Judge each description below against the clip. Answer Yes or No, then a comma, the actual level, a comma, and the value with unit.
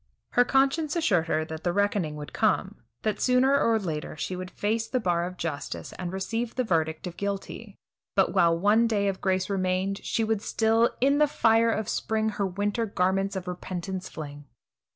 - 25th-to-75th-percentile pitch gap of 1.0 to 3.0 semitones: No, average, 4.0 semitones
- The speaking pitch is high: Yes, high, 200 Hz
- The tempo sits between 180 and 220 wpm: Yes, average, 190 wpm